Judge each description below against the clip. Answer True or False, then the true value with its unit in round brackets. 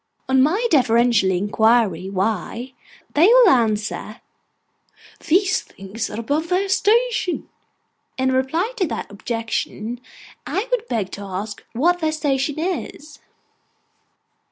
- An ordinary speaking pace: False (115 wpm)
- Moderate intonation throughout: False (8.4 semitones)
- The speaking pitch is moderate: False (260 Hz)